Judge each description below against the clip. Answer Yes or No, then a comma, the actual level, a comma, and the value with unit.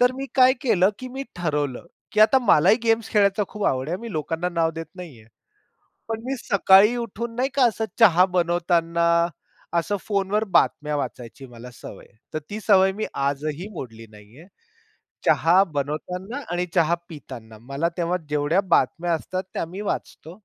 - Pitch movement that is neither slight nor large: No, wide, 5.8 semitones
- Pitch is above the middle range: No, medium, 175 Hz